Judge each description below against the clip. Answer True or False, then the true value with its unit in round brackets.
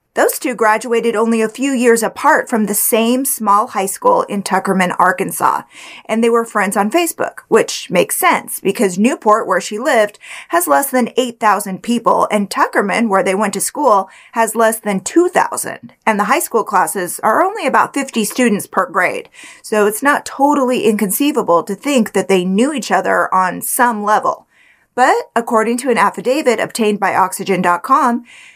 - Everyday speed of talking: True (170 wpm)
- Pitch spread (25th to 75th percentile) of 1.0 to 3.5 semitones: False (4.2 semitones)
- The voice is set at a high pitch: True (225 Hz)